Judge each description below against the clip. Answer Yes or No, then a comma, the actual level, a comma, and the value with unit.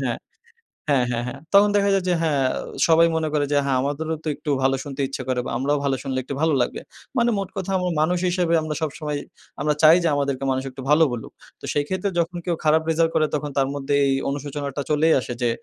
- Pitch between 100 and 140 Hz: No, medium, 150 Hz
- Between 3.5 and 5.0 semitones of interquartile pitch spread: No, average, 3.0 semitones